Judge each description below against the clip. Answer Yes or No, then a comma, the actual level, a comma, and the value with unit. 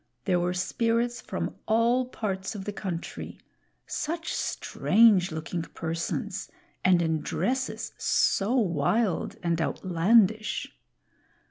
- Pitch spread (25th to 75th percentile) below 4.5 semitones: No, average, 4.9 semitones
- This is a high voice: Yes, high, 195 Hz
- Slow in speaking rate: Yes, slow, 105 wpm